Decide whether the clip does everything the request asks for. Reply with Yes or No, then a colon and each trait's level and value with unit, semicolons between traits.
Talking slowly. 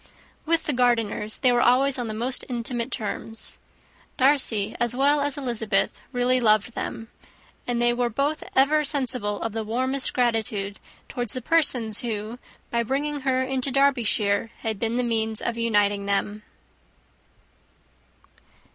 No: average, 145 wpm